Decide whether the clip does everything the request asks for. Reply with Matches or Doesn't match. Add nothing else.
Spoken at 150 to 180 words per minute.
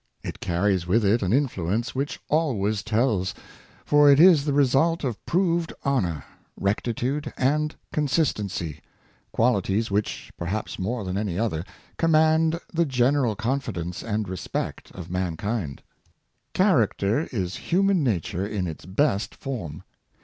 Doesn't match